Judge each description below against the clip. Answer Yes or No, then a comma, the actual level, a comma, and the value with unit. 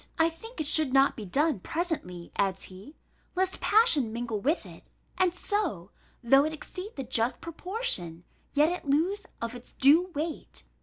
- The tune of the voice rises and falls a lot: Yes, wide, 7.3 semitones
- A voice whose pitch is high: Yes, very high, 300 Hz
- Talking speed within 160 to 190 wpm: Yes, average, 165 wpm